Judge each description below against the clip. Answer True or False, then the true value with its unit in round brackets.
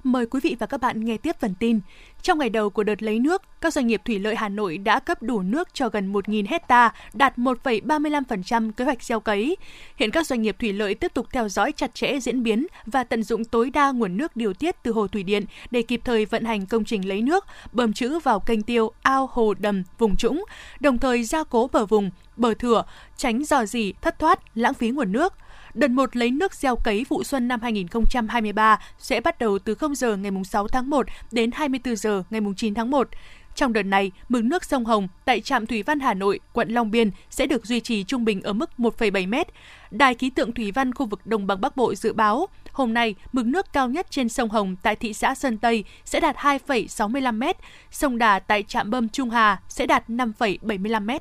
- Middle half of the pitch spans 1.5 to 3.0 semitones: False (3.7 semitones)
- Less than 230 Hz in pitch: False (235 Hz)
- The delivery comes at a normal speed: True (225 wpm)